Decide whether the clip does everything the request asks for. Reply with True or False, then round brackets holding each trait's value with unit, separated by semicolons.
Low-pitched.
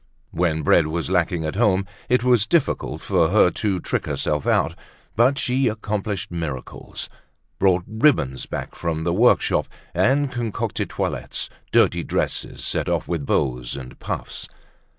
True (95 Hz)